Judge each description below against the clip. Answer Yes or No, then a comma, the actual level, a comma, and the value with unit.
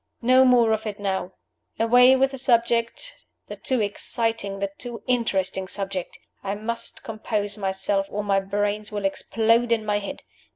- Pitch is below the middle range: No, high, 215 Hz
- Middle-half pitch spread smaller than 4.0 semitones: Yes, average, 2.9 semitones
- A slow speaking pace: No, average, 160 wpm